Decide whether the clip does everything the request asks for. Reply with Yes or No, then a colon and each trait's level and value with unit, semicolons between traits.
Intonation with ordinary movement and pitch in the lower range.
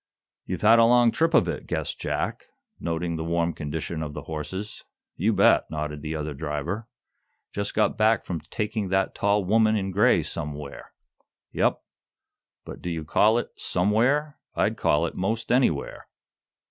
No: wide, 5.7 semitones; very low, 90 Hz